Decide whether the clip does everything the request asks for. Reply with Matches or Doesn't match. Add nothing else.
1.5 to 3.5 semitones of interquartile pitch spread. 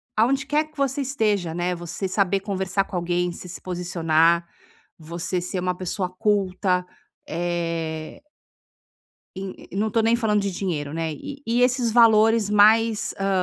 Doesn't match